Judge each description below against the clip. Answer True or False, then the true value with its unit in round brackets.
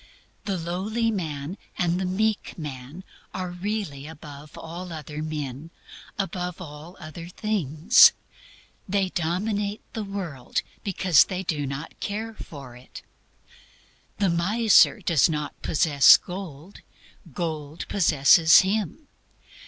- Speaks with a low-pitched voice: False (170 Hz)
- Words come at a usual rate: False (115 wpm)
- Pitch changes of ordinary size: True (4.6 semitones)